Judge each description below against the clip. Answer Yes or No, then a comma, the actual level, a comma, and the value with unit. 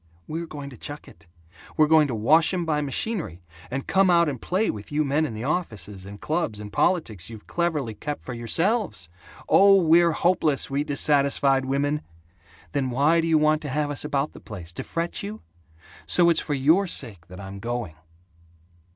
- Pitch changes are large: Yes, wide, 5.9 semitones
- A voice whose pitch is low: No, medium, 145 Hz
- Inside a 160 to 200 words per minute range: Yes, average, 190 wpm